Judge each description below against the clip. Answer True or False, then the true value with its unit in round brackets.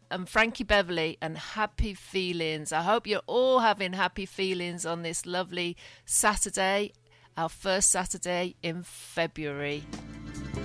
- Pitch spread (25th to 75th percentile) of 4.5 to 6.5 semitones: False (3.5 semitones)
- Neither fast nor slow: False (125 wpm)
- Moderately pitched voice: True (180 Hz)